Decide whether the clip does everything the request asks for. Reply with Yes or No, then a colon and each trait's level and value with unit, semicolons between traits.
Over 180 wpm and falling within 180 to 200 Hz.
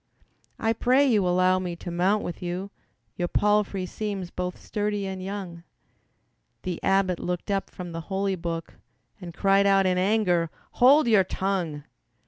No: average, 155 wpm; high, 190 Hz